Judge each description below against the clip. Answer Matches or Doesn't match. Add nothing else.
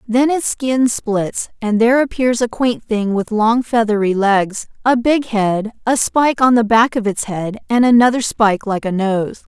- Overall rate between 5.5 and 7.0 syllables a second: Doesn't match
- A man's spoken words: Doesn't match